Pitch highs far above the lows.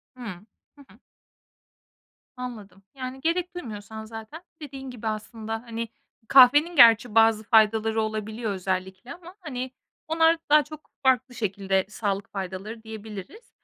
No: average, 4.0 semitones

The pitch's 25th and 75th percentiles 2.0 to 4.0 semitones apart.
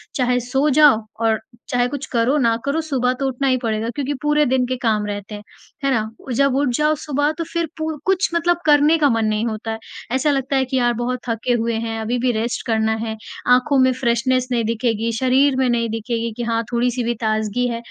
Yes: average, 3.3 semitones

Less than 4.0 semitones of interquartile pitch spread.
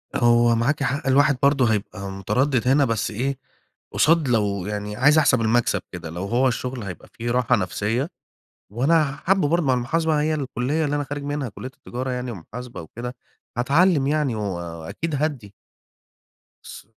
No: average, 4.6 semitones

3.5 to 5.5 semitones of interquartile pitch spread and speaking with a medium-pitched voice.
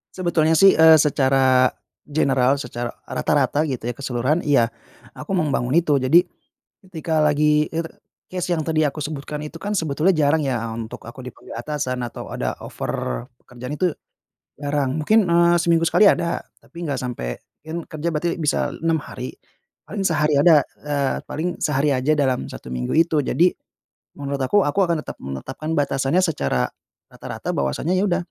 Yes: average, 3.8 semitones; medium, 150 Hz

